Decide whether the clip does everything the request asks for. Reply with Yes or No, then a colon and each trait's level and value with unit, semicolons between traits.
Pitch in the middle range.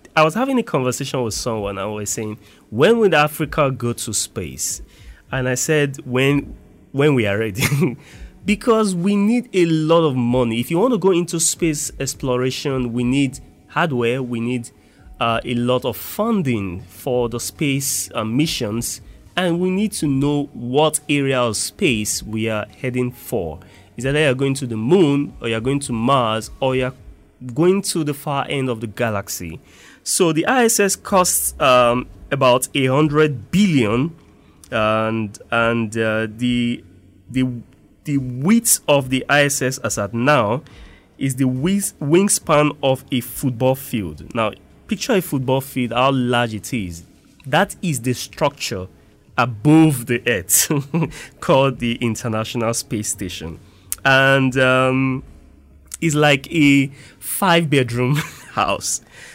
No: low, 130 Hz